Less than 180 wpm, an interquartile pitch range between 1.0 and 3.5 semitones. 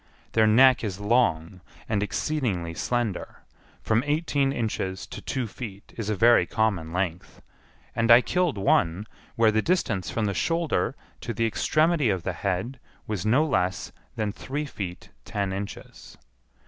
No: average, 150 wpm; average, 4.9 semitones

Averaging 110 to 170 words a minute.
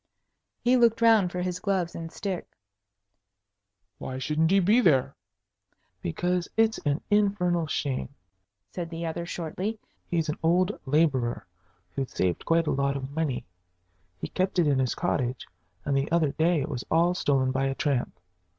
Yes: average, 160 wpm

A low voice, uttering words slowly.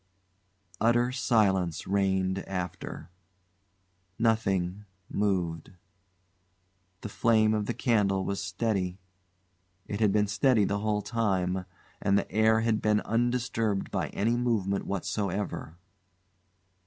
Yes: low, 105 Hz; slow, 105 wpm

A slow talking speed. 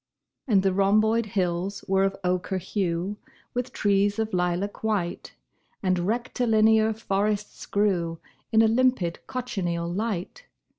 Yes: slow, 120 wpm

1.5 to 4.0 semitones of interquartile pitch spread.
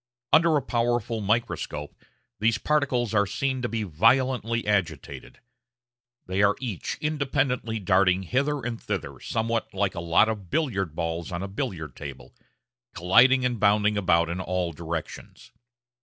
No: average, 5.3 semitones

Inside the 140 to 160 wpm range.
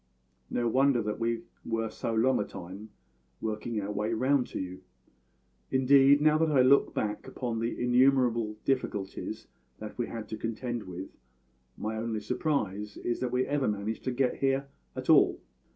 No: average, 170 wpm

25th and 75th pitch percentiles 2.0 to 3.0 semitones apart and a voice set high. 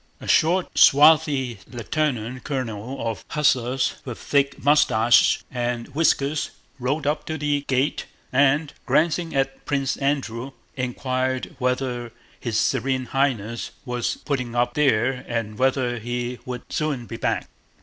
No: average, 2.7 semitones; low, 130 Hz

